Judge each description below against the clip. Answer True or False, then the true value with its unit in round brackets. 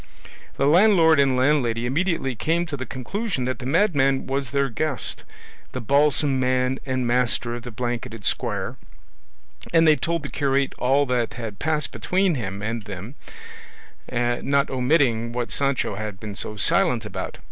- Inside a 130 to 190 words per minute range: True (160 wpm)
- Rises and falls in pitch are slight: False (3.5 semitones)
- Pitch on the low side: True (130 Hz)